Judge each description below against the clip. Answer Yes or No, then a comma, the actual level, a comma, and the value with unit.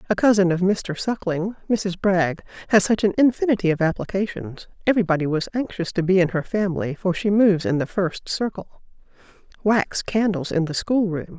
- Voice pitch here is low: No, high, 190 Hz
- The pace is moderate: Yes, average, 180 wpm